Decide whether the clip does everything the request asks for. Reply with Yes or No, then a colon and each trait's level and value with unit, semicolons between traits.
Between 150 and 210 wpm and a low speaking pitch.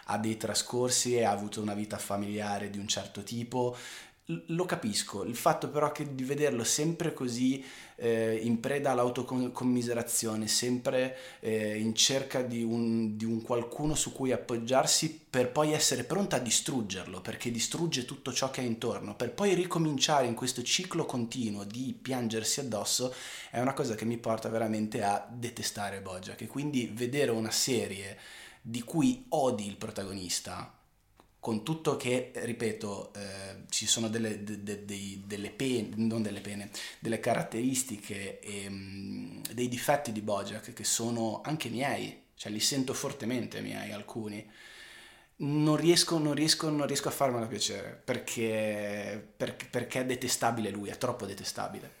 Yes: average, 155 wpm; low, 120 Hz